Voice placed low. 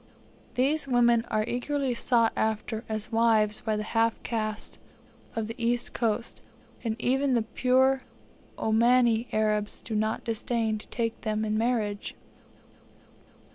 No: high, 230 Hz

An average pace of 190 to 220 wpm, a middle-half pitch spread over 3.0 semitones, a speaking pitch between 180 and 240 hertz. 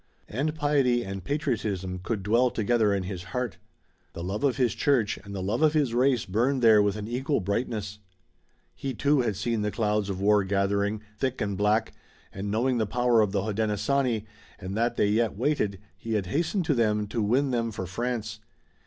No: average, 195 wpm; average, 3.6 semitones; low, 110 Hz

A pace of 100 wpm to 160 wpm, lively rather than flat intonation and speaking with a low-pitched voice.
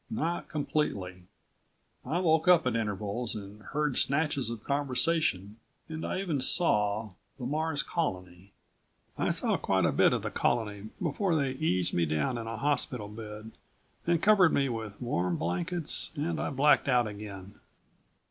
Yes: average, 155 wpm; wide, 7.1 semitones; low, 125 Hz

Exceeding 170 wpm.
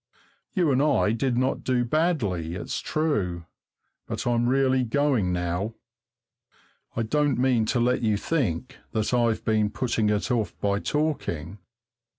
No: average, 145 wpm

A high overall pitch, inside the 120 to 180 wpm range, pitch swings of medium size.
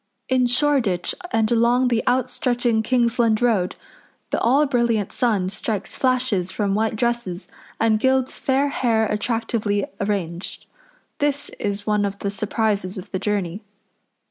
Yes: high, 225 Hz; average, 140 wpm; average, 3.3 semitones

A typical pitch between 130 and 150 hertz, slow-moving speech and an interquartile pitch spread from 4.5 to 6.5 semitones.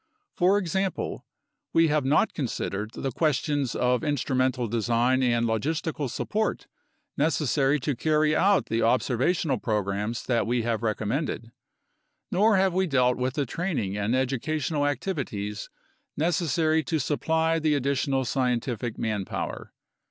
Yes: low, 135 Hz; slow, 125 wpm; average, 5.1 semitones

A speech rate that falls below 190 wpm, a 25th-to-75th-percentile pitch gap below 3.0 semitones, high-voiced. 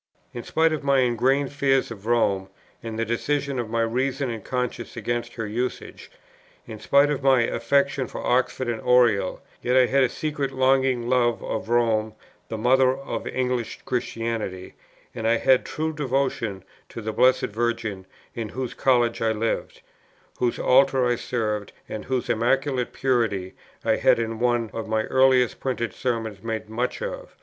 No: average, 170 wpm; narrow, 2.6 semitones; low, 120 Hz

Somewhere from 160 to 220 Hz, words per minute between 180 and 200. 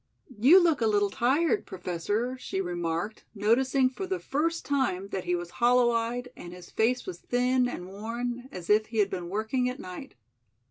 No: high, 230 Hz; average, 185 wpm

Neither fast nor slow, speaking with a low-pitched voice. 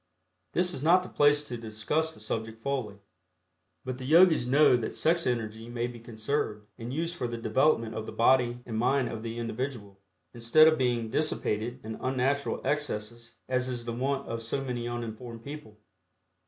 Yes: average, 180 wpm; low, 120 Hz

